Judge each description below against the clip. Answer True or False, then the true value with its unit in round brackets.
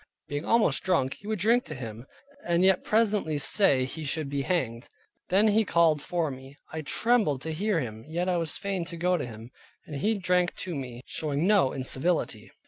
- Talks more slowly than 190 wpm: False (200 wpm)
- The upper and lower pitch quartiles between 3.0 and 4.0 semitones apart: False (5.5 semitones)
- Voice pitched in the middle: True (165 Hz)